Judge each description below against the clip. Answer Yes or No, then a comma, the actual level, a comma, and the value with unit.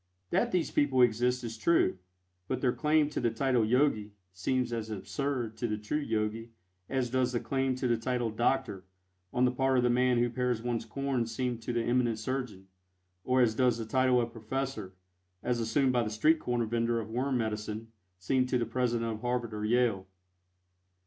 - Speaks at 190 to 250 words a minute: Yes, average, 195 wpm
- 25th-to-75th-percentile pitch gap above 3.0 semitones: No, narrow, 2.4 semitones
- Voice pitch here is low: Yes, low, 120 Hz